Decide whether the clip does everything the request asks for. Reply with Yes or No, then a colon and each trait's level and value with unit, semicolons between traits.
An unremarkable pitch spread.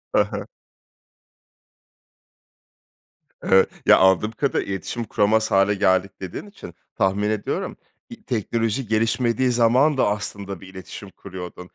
Yes: average, 3.6 semitones